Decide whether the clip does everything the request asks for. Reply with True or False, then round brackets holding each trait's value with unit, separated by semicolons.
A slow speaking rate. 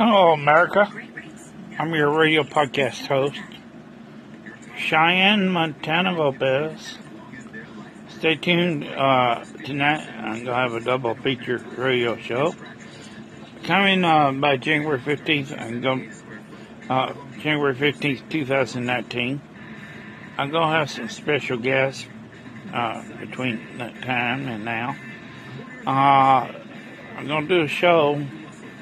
True (105 wpm)